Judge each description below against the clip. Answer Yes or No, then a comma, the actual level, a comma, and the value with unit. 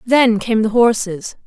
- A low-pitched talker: No, high, 225 Hz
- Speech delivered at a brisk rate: No, average, 165 wpm